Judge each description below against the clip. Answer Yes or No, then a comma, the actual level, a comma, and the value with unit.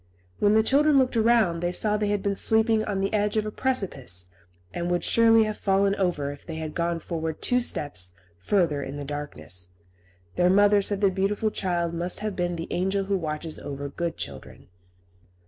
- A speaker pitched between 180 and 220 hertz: Yes, high, 190 Hz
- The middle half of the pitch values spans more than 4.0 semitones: Yes, average, 4.8 semitones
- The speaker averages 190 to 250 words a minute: Yes, average, 195 wpm